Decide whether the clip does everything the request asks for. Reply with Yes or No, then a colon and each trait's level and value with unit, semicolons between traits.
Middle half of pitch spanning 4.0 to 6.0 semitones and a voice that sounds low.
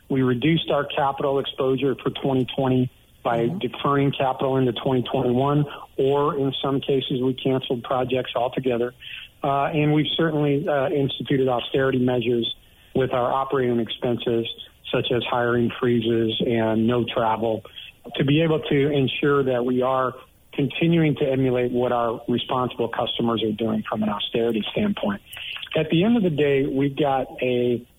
No: average, 2.8 semitones; low, 130 Hz